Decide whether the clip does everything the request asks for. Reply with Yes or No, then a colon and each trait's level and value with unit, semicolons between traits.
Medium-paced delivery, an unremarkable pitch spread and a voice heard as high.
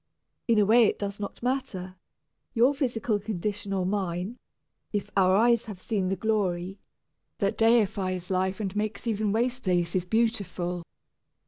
Yes: average, 150 wpm; average, 3.2 semitones; high, 205 Hz